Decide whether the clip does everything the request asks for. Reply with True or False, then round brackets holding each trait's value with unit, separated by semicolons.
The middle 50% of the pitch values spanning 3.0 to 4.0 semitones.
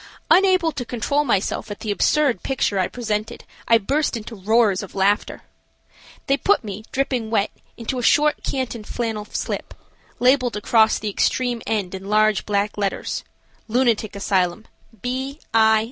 True (3.6 semitones)